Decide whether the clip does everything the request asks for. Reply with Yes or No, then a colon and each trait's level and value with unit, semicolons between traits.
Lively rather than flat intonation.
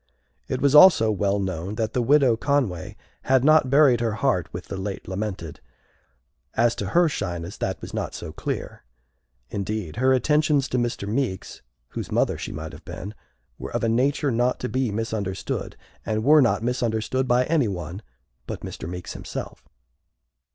No: average, 5.0 semitones